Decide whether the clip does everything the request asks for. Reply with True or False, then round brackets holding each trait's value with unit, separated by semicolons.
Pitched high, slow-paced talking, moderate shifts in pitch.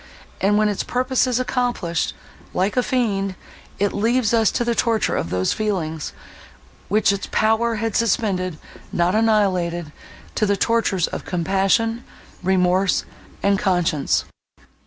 True (200 Hz; 125 wpm; 3.8 semitones)